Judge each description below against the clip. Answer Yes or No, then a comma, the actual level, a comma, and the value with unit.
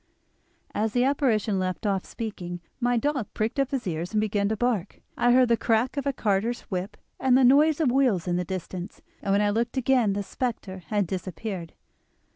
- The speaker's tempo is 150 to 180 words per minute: No, average, 200 wpm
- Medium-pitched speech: No, high, 220 Hz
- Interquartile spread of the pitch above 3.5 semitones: Yes, average, 4.6 semitones